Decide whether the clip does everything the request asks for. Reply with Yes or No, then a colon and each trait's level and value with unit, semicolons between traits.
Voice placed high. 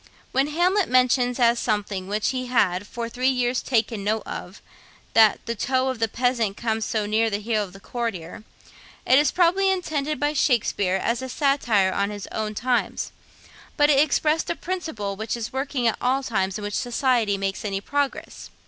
Yes: high, 235 Hz